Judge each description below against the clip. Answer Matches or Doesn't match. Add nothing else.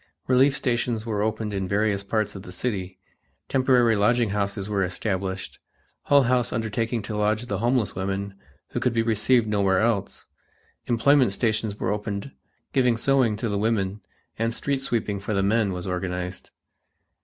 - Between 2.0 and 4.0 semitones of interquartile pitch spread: Matches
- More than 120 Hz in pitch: Doesn't match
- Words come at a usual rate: Matches